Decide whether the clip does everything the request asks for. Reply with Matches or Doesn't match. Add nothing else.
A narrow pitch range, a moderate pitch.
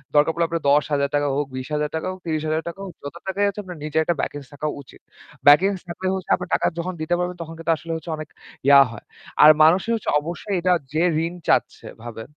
Doesn't match